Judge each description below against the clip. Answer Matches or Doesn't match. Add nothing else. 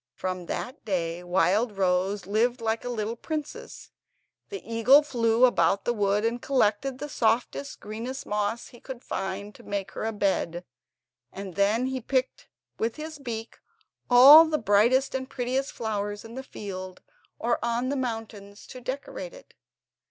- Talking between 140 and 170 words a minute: Matches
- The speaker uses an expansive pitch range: Doesn't match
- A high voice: Matches